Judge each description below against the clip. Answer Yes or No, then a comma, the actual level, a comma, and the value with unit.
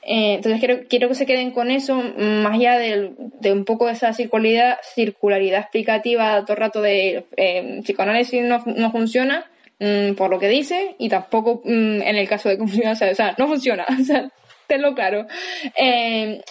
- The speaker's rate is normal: Yes, average, 180 wpm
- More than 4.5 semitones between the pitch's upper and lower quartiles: No, average, 3.0 semitones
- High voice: Yes, high, 225 Hz